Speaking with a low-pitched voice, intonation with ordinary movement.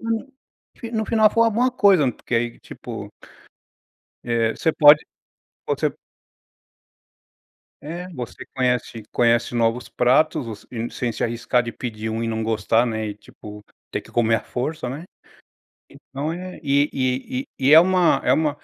No: low, 125 Hz; wide, 6.4 semitones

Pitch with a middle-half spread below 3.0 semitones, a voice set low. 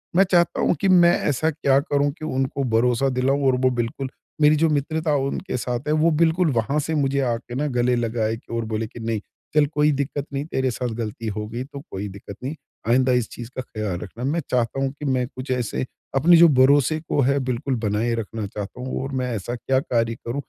No: average, 3.7 semitones; low, 130 Hz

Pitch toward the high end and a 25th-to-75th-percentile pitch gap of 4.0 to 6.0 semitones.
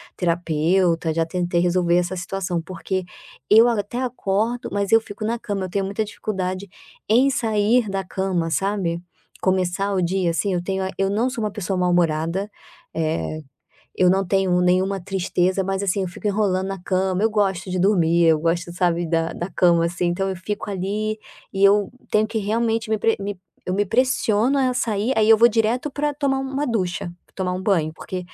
No: high, 195 Hz; average, 3.2 semitones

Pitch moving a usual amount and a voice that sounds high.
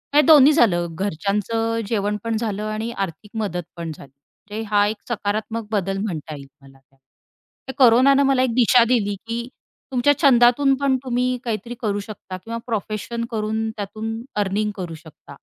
Yes: average, 3.2 semitones; high, 215 Hz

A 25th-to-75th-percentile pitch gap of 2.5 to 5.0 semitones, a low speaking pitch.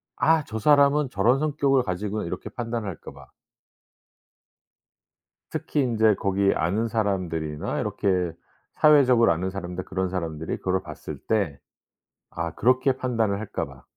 No: wide, 5.4 semitones; low, 105 Hz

